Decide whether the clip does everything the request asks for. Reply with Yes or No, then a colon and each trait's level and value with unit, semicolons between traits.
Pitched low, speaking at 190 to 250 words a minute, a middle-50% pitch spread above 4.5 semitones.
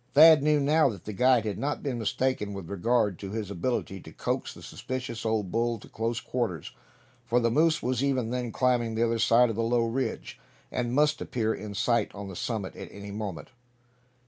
No: low, 115 Hz; fast, 205 wpm; average, 3.3 semitones